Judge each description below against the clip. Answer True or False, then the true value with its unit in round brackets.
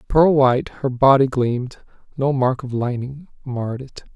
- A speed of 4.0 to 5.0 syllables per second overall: True (4.7 syllables/s)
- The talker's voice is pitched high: False (130 Hz)